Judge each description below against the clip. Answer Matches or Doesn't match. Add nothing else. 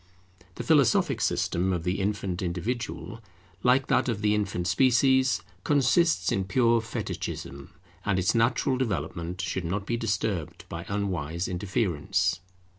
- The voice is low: Matches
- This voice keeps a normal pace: Doesn't match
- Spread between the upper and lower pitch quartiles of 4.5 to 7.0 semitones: Matches